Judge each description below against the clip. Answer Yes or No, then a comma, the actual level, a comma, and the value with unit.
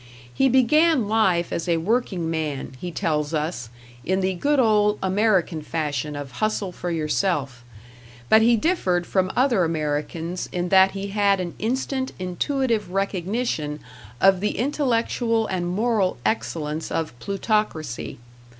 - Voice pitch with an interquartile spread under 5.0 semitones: No, wide, 5.4 semitones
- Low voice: No, medium, 185 Hz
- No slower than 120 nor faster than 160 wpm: Yes, slow, 135 wpm